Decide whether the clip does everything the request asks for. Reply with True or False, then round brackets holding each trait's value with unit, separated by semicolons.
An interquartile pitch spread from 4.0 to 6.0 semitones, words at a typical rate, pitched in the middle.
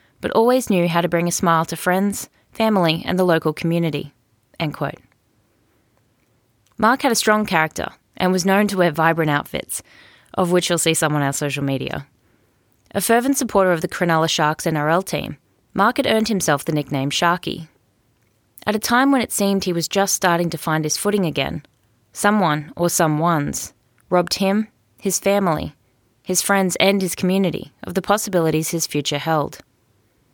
True (5.3 semitones; 175 wpm; 165 Hz)